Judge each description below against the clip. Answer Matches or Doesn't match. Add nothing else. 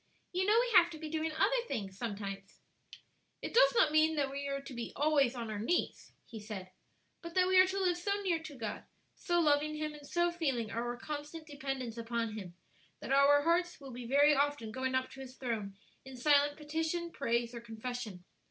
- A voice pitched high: Matches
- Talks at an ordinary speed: Doesn't match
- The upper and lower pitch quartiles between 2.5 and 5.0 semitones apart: Doesn't match